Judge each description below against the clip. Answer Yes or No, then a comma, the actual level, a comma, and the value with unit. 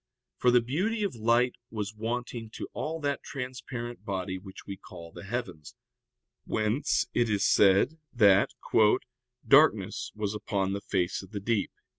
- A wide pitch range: No, average, 3.8 semitones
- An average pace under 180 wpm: Yes, average, 150 wpm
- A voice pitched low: Yes, low, 110 Hz